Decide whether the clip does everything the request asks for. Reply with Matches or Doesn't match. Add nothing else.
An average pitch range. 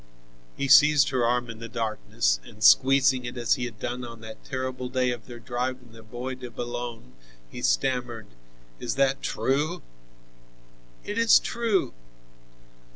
Doesn't match